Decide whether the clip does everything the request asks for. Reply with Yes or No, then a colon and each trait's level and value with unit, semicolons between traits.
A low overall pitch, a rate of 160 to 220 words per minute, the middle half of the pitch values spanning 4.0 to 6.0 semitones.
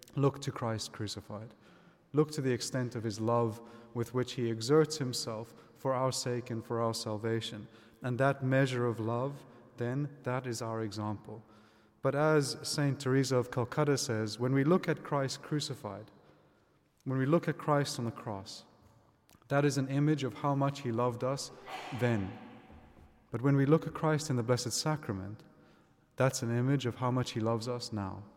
No: low, 125 Hz; average, 180 wpm; average, 3.6 semitones